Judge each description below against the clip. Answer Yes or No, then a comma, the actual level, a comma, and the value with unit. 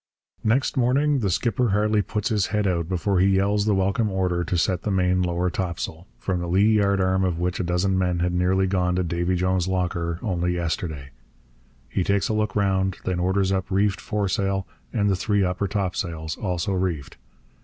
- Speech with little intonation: Yes, narrow, 2.2 semitones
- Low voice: Yes, very low, 95 Hz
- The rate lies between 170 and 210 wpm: Yes, average, 190 wpm